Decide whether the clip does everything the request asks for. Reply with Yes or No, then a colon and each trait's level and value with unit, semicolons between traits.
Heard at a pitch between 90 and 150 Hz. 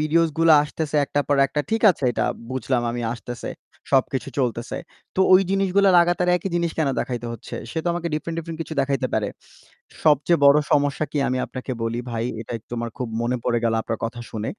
Yes: medium, 140 Hz